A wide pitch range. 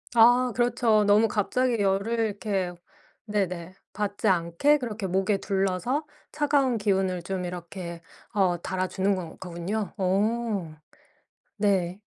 No: average, 3.5 semitones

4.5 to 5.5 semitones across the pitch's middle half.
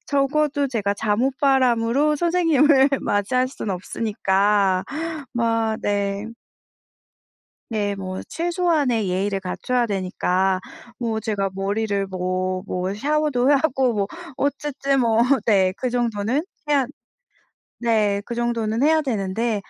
Yes: average, 5.2 semitones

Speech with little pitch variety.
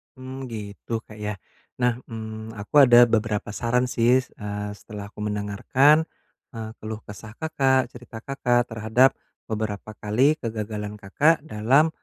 No: average, 3.4 semitones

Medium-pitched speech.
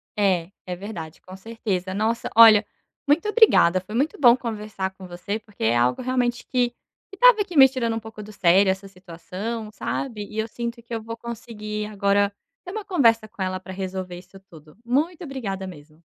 No: high, 210 Hz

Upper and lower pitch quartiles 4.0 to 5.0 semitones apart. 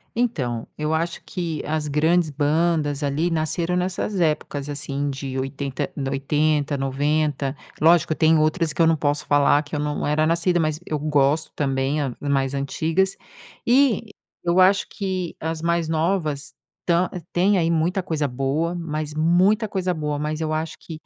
No: average, 2.9 semitones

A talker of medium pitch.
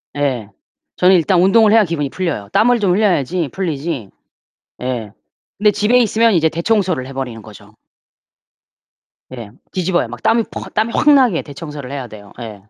Yes: medium, 165 Hz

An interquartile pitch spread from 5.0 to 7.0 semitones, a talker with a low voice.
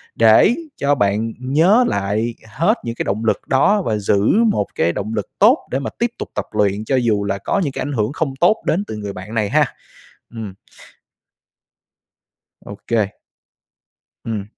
Yes: wide, 5.4 semitones; low, 115 Hz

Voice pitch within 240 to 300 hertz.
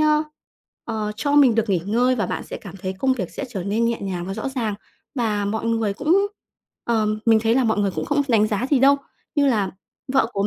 No: high, 225 Hz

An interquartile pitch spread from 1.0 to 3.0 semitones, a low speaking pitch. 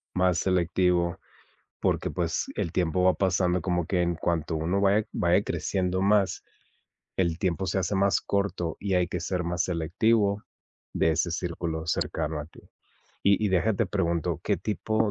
Yes: narrow, 2.4 semitones; very low, 90 Hz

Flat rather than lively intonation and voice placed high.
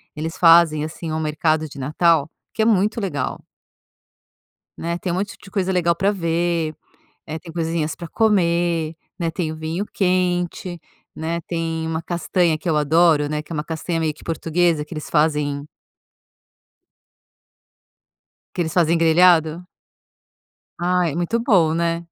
No: narrow, 1.9 semitones; medium, 165 Hz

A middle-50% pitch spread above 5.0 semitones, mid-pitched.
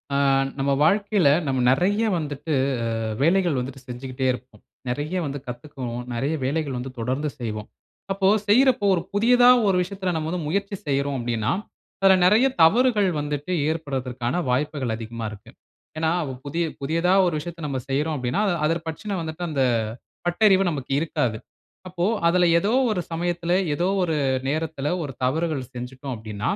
Yes: wide, 5.4 semitones; medium, 150 Hz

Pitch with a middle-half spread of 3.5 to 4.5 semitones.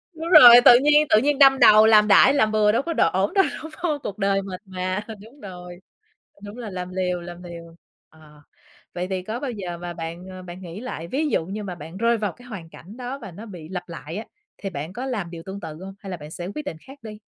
No: average, 5.2 semitones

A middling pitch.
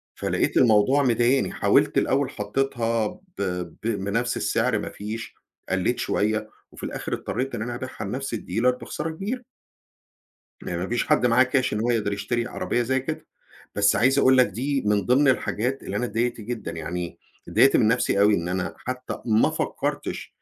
No: low, 120 Hz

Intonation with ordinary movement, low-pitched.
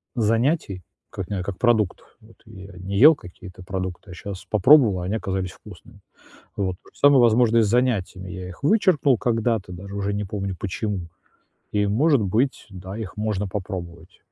Yes: average, 3.6 semitones; low, 100 Hz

